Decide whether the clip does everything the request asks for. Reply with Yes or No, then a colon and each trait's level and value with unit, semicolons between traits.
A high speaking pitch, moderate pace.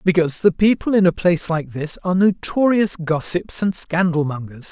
No: medium, 175 Hz; average, 180 wpm